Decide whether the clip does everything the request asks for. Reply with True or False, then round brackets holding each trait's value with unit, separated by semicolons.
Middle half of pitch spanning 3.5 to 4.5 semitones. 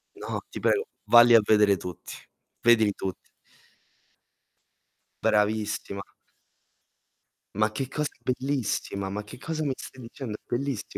True (4.0 semitones)